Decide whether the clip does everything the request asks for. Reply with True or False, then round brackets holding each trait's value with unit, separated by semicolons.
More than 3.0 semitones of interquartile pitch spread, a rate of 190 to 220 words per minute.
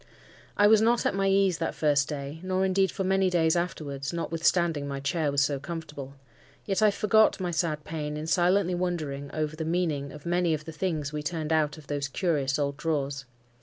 True (3.8 semitones; 205 wpm)